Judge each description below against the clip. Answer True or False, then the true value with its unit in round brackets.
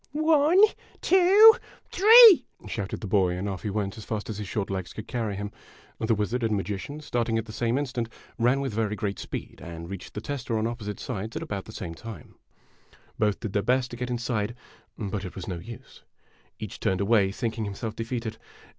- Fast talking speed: True (210 wpm)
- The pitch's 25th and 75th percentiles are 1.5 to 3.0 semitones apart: False (3.4 semitones)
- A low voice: True (110 Hz)